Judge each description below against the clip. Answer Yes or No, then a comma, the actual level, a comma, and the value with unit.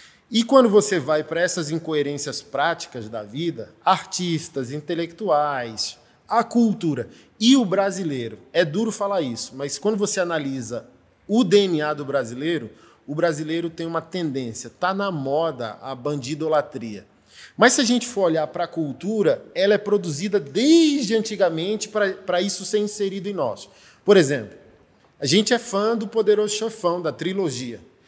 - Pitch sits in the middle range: Yes, medium, 170 Hz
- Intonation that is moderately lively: No, wide, 5.9 semitones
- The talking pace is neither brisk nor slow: Yes, average, 150 wpm